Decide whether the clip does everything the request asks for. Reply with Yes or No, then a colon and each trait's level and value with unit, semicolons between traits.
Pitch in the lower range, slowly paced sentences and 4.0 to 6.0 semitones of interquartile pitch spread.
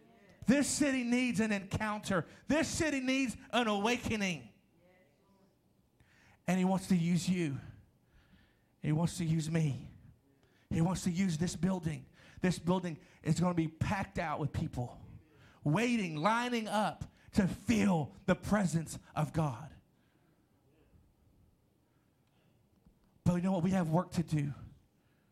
No: medium, 175 Hz; slow, 130 wpm; average, 5.1 semitones